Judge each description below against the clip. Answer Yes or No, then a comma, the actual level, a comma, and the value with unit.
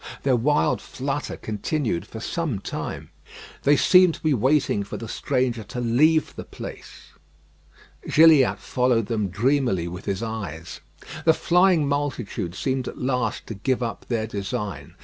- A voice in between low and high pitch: No, low, 125 Hz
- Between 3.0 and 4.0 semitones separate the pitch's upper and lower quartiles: No, average, 5.0 semitones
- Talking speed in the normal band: Yes, average, 150 wpm